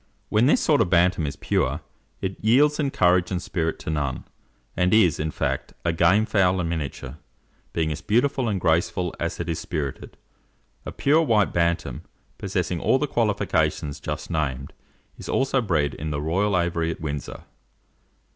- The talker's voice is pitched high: No, very low, 85 Hz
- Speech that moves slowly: No, average, 170 wpm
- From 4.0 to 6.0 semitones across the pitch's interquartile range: Yes, average, 4.9 semitones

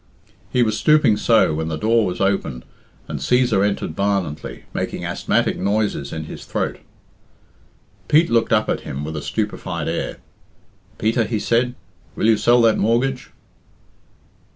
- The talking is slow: No, average, 150 wpm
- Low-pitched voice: Yes, low, 105 Hz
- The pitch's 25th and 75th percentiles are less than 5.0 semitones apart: No, wide, 5.6 semitones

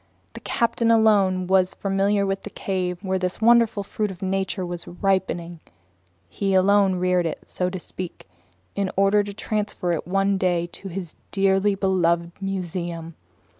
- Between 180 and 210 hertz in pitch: Yes, high, 190 Hz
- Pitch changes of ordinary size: No, narrow, 1.8 semitones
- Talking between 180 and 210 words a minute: No, average, 155 wpm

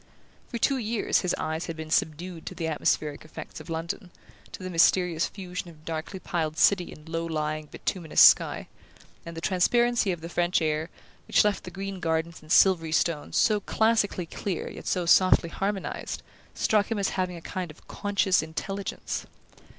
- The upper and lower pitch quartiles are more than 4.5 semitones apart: No, average, 3.3 semitones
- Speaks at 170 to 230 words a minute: Yes, average, 175 wpm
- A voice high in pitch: No, medium, 175 Hz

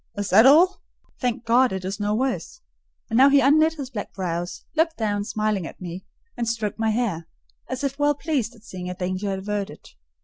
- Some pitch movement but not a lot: No, wide, 5.7 semitones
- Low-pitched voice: No, high, 220 Hz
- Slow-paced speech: No, average, 200 wpm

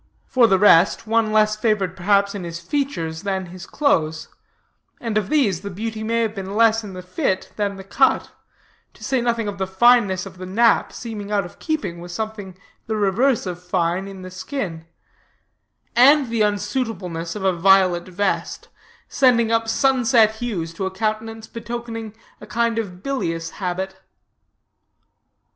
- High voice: Yes, high, 205 Hz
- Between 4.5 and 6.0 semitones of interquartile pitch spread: No, average, 3.6 semitones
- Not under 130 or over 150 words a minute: No, average, 165 wpm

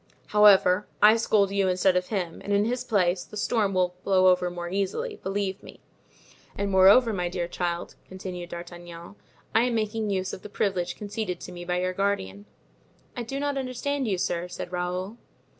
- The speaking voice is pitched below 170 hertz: No, high, 190 Hz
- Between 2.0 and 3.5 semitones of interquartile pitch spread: Yes, average, 2.8 semitones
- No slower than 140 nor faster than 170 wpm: No, average, 185 wpm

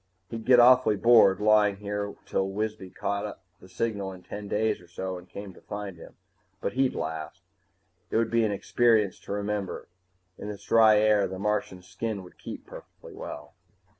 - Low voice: Yes, low, 105 Hz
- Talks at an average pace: Yes, average, 180 wpm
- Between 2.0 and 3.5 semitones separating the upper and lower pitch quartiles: Yes, narrow, 2.4 semitones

